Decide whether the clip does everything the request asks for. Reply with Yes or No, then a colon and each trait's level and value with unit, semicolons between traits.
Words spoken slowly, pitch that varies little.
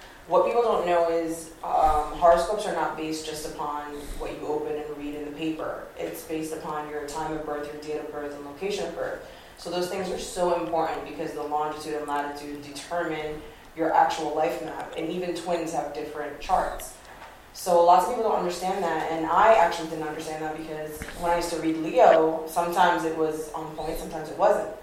No: fast, 205 wpm; narrow, 2.2 semitones